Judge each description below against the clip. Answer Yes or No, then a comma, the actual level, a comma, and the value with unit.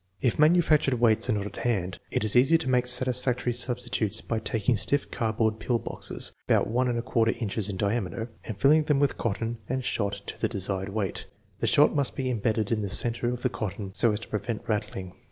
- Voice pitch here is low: Yes, low, 115 Hz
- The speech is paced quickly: Yes, fast, 210 wpm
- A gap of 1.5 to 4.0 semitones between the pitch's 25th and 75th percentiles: Yes, average, 3.2 semitones